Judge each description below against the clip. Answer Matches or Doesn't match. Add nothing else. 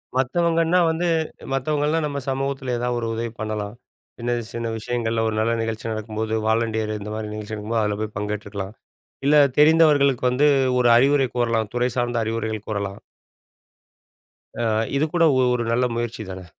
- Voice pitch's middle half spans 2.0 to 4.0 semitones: Matches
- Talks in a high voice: Doesn't match